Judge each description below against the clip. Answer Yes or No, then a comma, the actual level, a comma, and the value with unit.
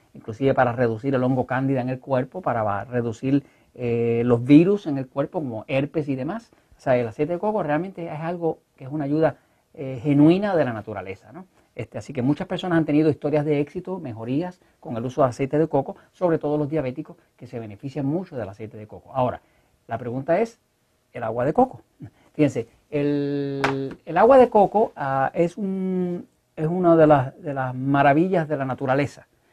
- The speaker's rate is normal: No, fast, 195 wpm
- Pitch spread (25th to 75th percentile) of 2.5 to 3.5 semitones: No, average, 4.2 semitones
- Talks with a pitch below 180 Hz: Yes, medium, 140 Hz